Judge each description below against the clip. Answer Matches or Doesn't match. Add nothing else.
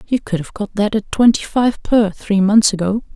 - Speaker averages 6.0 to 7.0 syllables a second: Doesn't match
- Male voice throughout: Doesn't match